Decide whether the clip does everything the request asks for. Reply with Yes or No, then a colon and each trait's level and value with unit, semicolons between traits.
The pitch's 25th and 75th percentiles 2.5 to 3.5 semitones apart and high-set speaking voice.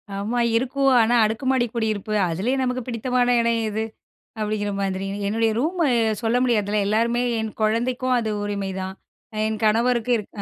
Yes: average, 2.8 semitones; high, 225 Hz